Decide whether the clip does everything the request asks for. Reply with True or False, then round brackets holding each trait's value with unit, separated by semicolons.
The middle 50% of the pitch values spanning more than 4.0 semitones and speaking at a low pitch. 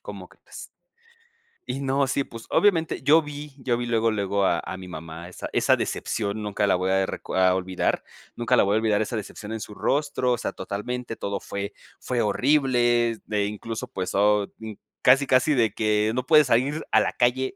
True (4.4 semitones; 115 Hz)